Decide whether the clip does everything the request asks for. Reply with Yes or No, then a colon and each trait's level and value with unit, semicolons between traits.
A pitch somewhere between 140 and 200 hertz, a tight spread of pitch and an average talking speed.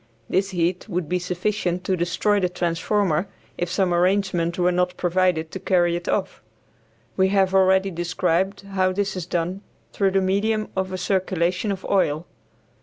Yes: medium, 185 Hz; narrow, 1.7 semitones; average, 165 wpm